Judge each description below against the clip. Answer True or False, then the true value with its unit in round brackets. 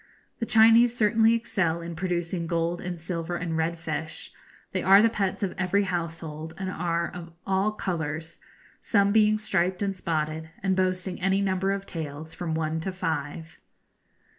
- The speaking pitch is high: False (180 Hz)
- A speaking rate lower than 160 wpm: False (165 wpm)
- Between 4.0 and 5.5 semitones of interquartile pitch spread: False (3.2 semitones)